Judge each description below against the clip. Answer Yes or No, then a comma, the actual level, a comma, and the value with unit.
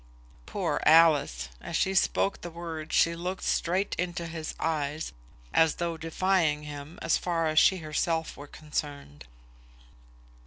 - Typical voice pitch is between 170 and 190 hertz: No, medium, 160 Hz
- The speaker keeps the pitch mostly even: Yes, narrow, 2.2 semitones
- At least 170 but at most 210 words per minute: No, average, 140 wpm